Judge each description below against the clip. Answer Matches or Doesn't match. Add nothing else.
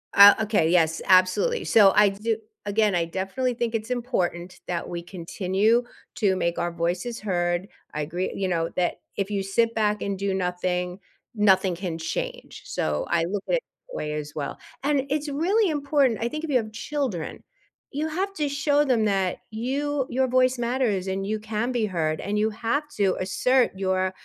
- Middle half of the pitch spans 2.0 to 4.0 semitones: Doesn't match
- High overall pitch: Matches